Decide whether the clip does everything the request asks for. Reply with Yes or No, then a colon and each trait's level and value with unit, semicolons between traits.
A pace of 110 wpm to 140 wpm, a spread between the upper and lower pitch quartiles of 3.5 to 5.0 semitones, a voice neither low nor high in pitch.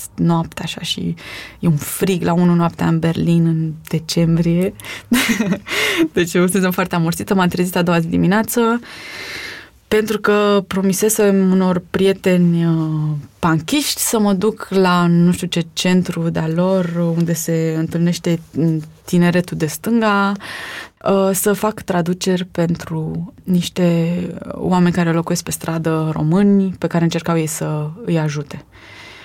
No: average, 135 wpm; average, 2.9 semitones; medium, 175 Hz